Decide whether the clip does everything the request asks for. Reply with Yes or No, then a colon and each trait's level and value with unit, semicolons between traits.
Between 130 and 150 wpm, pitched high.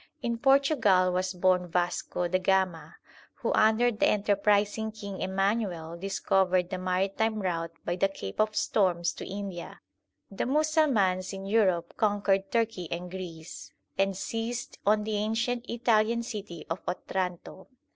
Yes: average, 140 wpm; high, 195 Hz